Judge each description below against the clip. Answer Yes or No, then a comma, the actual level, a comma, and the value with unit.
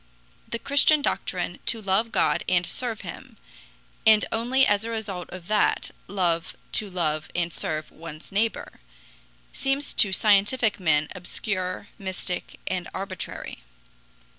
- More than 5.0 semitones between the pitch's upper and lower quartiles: No, average, 4.0 semitones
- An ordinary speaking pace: No, slow, 130 wpm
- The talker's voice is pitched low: No, high, 195 Hz